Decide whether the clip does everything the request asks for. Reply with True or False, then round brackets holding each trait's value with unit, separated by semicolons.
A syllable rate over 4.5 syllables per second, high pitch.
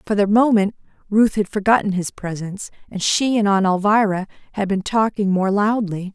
True (5.2 syllables/s; 205 Hz)